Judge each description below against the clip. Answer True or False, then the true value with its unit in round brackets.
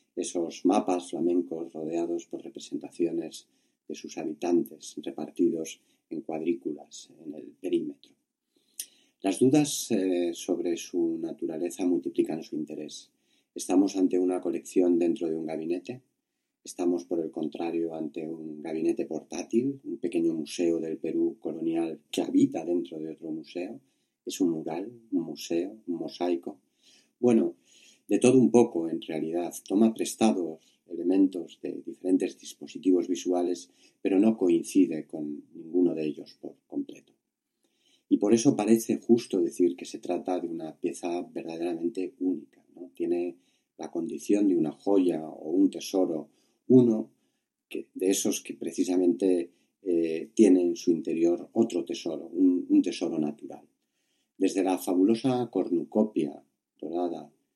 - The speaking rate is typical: False (130 wpm)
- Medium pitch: False (290 Hz)